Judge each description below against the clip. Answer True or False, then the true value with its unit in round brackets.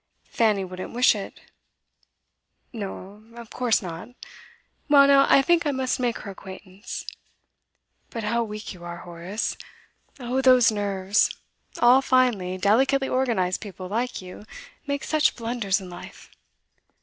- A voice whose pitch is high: True (220 Hz)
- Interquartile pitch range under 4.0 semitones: False (5.0 semitones)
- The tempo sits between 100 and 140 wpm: True (135 wpm)